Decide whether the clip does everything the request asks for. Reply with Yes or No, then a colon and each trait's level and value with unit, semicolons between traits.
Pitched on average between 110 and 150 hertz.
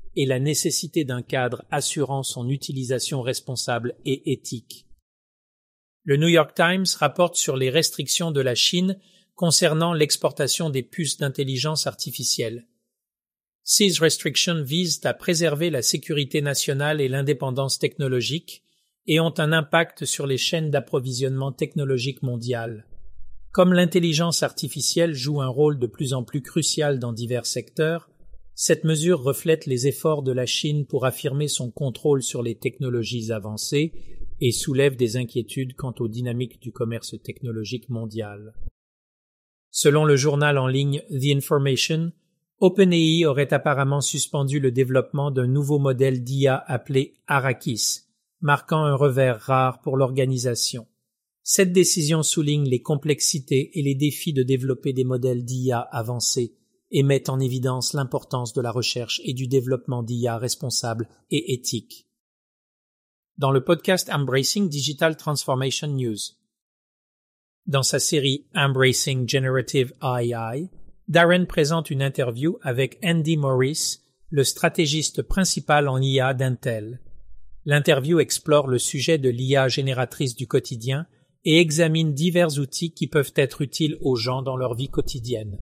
Yes: medium, 140 Hz